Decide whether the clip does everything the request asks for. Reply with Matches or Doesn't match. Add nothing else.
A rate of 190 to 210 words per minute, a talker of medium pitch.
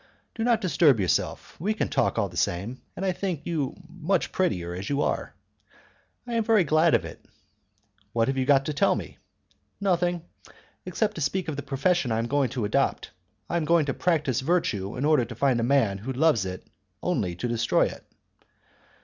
Matches